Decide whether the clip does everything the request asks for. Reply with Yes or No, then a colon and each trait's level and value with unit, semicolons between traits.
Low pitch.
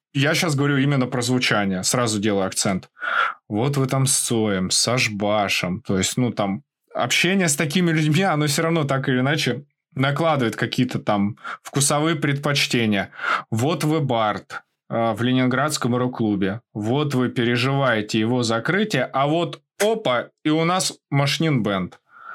Yes: low, 130 Hz